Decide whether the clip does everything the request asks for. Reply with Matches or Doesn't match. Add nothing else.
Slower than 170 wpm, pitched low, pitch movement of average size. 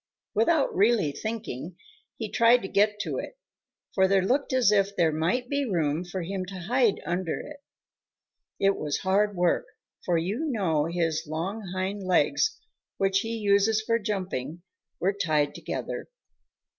Doesn't match